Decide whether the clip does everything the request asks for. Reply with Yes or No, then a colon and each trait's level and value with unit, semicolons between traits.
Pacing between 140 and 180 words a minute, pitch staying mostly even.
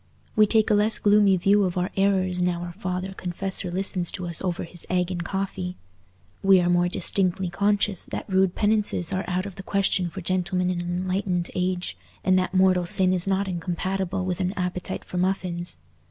No: average, 195 wpm; narrow, 1.5 semitones